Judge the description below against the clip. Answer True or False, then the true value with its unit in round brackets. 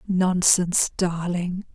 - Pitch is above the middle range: False (180 Hz)